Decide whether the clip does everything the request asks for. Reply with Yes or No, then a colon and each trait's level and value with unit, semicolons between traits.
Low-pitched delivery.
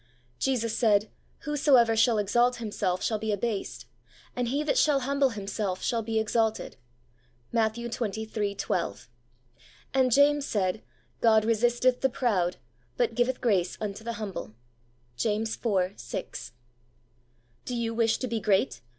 No: high, 220 Hz